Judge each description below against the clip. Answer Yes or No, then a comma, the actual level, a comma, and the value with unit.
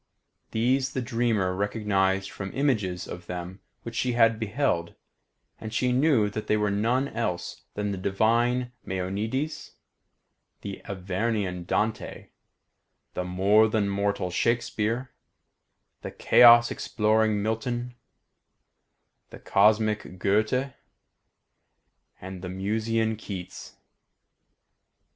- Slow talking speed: Yes, slow, 105 wpm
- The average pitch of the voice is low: Yes, low, 110 Hz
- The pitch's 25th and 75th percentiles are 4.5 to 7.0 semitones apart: No, average, 3.5 semitones